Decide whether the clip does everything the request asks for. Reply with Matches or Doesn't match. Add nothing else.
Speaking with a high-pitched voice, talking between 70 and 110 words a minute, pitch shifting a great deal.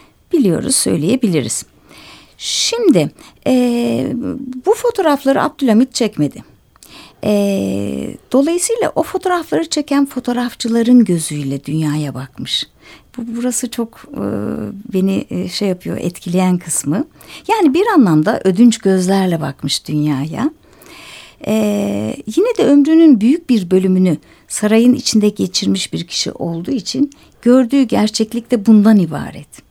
Matches